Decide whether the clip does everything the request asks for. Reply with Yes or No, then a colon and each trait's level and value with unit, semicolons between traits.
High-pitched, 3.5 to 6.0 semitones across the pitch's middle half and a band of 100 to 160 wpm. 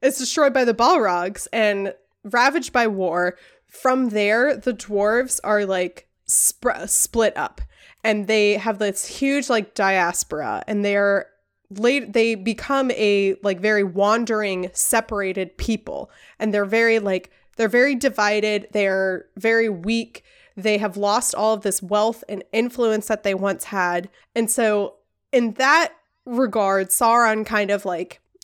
No: high, 215 Hz; average, 3.1 semitones; average, 145 wpm